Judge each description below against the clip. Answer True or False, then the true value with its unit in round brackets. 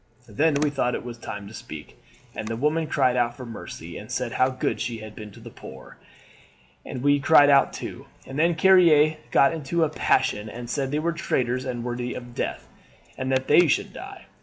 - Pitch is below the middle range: True (130 Hz)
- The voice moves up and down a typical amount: True (4.1 semitones)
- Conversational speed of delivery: False (215 wpm)